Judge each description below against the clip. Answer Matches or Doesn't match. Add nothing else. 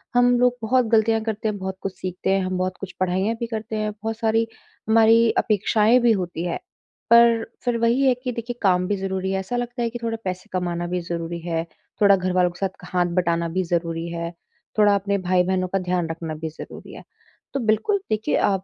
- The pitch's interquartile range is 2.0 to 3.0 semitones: Doesn't match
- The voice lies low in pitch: Doesn't match